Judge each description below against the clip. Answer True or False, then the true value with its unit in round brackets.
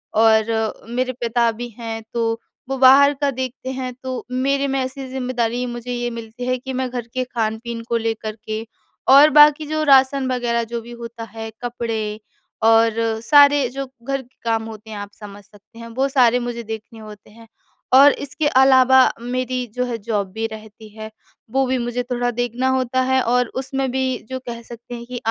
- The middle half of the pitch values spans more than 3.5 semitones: False (2.4 semitones)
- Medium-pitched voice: False (245 Hz)